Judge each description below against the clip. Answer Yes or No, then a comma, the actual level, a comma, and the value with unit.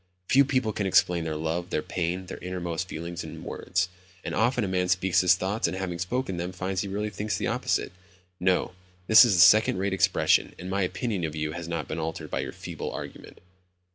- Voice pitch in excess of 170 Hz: No, very low, 90 Hz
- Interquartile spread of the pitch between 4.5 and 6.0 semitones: No, narrow, 2.5 semitones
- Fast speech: Yes, fast, 210 wpm